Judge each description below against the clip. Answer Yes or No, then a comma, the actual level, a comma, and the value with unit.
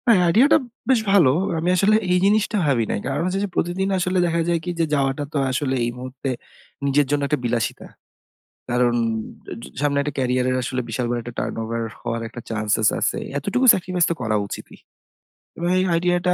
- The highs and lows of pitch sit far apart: Yes, wide, 6.4 semitones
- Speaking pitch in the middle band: Yes, medium, 145 Hz